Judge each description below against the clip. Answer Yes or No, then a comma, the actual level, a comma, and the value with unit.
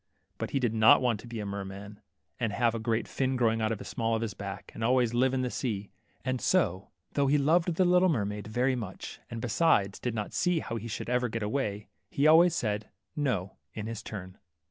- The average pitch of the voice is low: Yes, low, 115 Hz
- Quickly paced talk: Yes, fast, 235 wpm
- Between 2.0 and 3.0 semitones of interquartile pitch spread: No, average, 4.0 semitones